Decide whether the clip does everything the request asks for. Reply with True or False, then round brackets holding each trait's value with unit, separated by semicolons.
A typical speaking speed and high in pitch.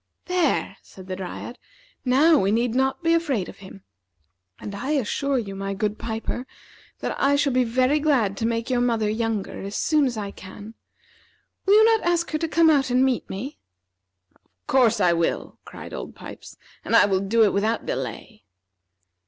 True (185 wpm; 235 Hz)